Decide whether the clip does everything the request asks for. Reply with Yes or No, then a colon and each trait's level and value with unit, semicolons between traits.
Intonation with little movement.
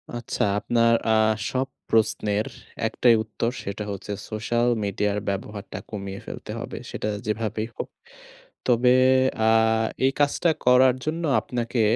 No: average, 3.1 semitones